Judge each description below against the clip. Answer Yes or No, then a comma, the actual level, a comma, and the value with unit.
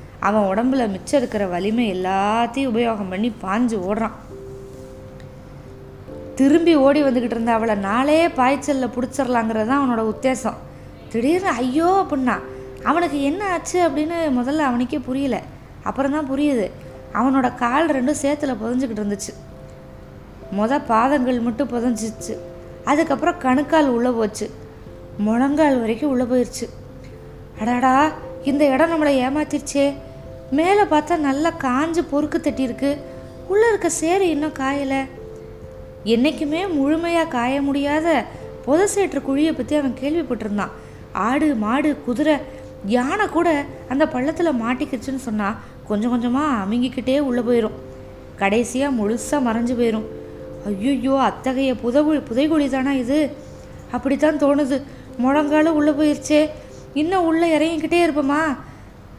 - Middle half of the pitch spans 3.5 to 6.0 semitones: Yes, average, 4.4 semitones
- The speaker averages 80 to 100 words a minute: No, average, 110 wpm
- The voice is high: Yes, very high, 270 Hz